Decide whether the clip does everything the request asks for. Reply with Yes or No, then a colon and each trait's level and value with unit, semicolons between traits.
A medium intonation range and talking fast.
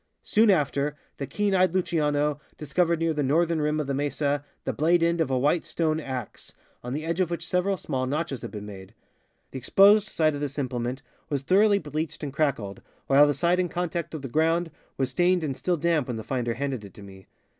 Yes: average, 4.1 semitones; fast, 220 wpm